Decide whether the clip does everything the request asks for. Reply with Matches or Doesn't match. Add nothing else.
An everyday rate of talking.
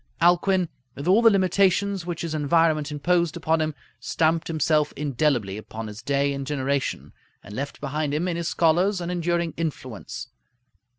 Matches